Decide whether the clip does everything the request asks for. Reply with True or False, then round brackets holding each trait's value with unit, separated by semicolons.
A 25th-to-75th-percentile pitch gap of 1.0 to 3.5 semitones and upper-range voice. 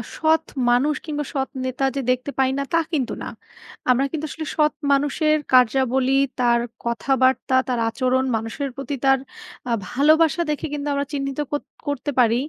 True (2.5 semitones; 270 Hz)